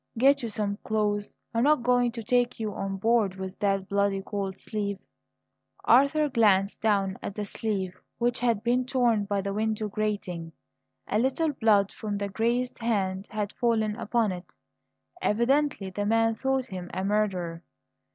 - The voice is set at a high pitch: Yes, high, 215 Hz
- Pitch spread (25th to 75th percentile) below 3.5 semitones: Yes, average, 3.1 semitones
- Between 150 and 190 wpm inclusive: Yes, average, 160 wpm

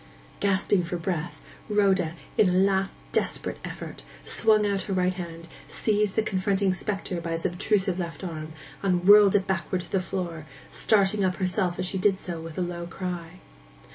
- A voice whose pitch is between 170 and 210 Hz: Yes, medium, 185 Hz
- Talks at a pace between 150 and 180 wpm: Yes, average, 175 wpm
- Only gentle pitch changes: Yes, narrow, 2.3 semitones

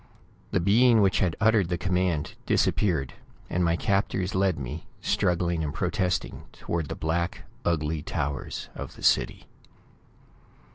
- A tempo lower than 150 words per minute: Yes, slow, 135 wpm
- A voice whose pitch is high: No, very low, 85 Hz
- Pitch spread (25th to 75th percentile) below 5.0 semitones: Yes, average, 2.9 semitones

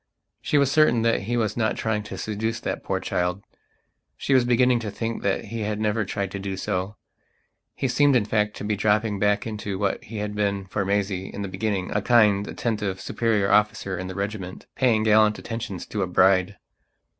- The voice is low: Yes, low, 105 Hz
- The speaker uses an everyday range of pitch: No, narrow, 2.3 semitones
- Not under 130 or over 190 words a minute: No, average, 200 wpm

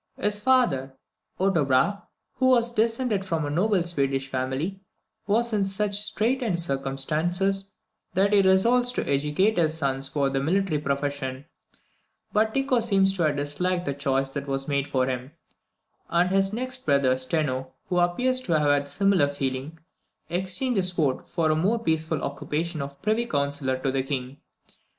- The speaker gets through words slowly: No, average, 165 wpm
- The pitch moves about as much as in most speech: No, wide, 6.3 semitones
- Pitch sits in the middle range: Yes, medium, 165 Hz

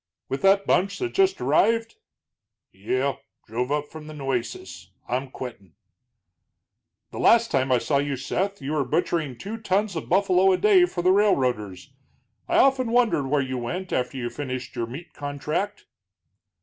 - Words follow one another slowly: No, average, 160 wpm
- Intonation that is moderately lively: No, wide, 7.5 semitones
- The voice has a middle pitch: Yes, medium, 150 Hz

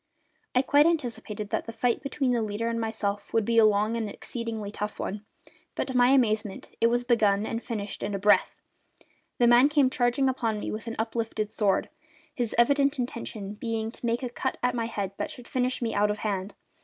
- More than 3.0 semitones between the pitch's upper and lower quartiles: No, average, 2.7 semitones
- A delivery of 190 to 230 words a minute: Yes, fast, 205 wpm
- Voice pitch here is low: No, high, 230 Hz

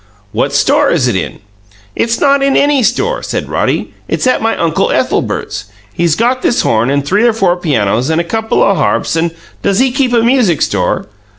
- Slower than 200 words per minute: No, fast, 205 wpm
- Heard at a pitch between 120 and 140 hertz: No, high, 200 Hz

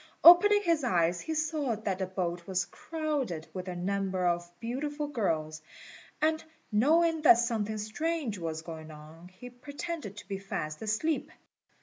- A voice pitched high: Yes, high, 215 Hz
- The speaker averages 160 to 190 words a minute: No, average, 150 wpm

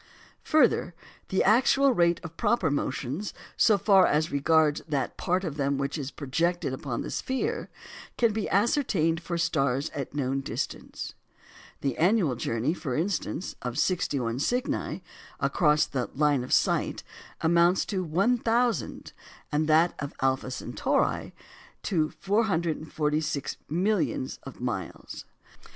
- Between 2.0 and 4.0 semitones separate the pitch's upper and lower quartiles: No, average, 5.3 semitones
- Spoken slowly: Yes, slow, 130 wpm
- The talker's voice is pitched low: No, medium, 160 Hz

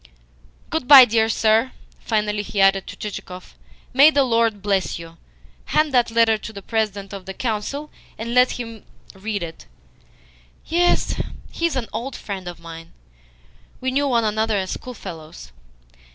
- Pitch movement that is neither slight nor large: Yes, average, 4.3 semitones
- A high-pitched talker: Yes, high, 220 Hz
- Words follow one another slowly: No, average, 155 wpm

